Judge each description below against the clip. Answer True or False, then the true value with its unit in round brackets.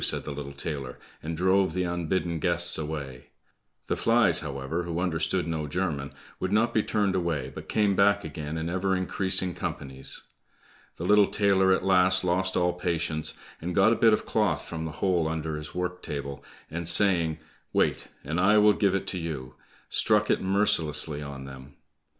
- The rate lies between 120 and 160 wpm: False (180 wpm)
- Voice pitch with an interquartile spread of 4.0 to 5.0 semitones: False (3.6 semitones)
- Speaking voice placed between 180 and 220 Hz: False (85 Hz)